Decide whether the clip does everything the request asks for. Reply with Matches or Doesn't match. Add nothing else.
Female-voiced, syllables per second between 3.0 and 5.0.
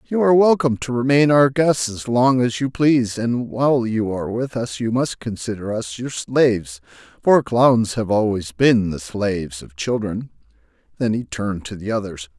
Doesn't match